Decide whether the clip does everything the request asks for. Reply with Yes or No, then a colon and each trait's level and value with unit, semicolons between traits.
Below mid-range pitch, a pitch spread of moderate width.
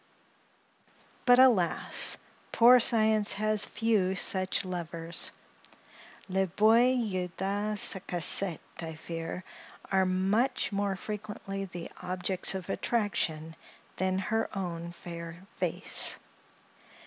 No: high, 190 Hz; average, 3.3 semitones